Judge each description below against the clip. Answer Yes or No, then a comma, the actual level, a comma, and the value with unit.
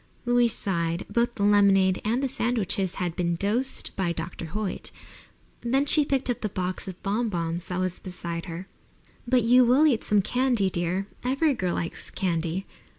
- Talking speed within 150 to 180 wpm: Yes, average, 175 wpm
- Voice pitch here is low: No, high, 200 Hz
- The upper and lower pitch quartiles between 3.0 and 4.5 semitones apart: No, average, 5.3 semitones